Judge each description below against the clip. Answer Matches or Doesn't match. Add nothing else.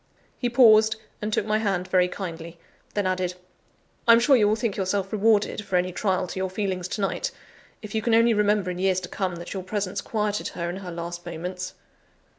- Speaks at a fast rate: Matches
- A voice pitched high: Matches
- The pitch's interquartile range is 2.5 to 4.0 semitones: Matches